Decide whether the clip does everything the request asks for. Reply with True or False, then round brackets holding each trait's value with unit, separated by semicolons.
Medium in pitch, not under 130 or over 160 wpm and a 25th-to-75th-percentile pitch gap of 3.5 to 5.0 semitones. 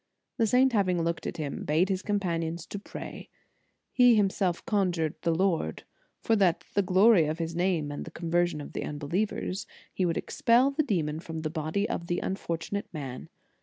False (175 Hz; 185 wpm; 3.8 semitones)